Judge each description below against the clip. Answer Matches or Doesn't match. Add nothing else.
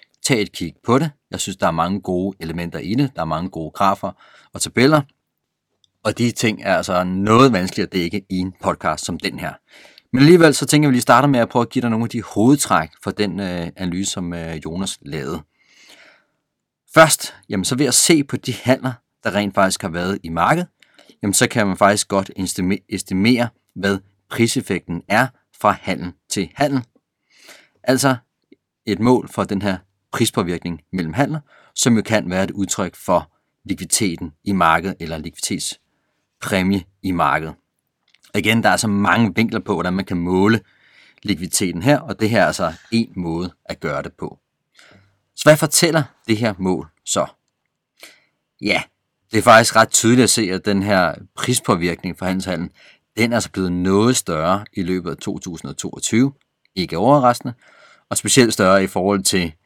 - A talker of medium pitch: Doesn't match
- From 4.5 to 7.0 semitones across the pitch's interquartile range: Matches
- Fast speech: Doesn't match